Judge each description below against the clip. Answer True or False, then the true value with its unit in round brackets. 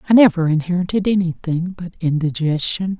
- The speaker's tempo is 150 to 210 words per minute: False (120 wpm)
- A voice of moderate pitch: True (175 Hz)